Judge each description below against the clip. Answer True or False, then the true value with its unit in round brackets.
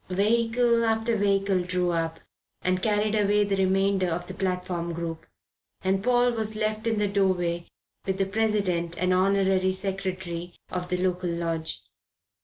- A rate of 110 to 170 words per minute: True (150 wpm)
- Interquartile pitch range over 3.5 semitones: False (2.6 semitones)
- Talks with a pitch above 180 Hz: True (190 Hz)